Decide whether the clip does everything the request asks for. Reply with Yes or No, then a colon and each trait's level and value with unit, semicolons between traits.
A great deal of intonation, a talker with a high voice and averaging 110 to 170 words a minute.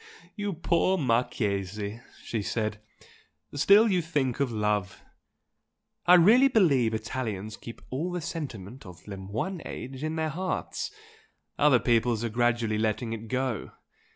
No: wide, 6.9 semitones; low, 120 Hz; slow, 135 wpm